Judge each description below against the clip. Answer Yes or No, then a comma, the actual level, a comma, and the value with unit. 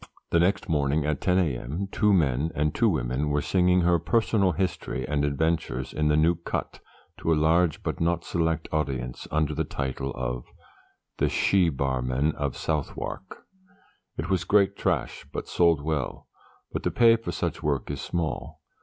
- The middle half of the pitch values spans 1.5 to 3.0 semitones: No, average, 3.8 semitones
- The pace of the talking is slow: No, average, 170 wpm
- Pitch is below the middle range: Yes, very low, 80 Hz